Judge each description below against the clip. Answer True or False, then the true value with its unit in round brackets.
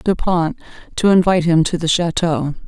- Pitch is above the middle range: False (170 Hz)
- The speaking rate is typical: True (180 wpm)